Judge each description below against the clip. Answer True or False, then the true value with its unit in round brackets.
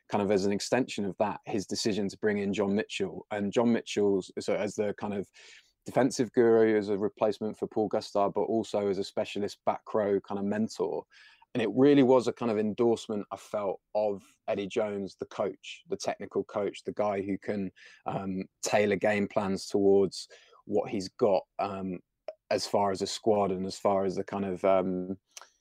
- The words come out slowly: False (195 wpm)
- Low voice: True (100 Hz)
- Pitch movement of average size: False (2.0 semitones)